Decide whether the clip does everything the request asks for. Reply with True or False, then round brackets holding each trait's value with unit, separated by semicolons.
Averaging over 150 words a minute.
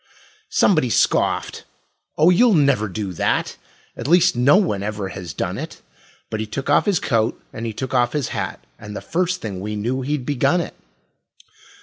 True (185 wpm)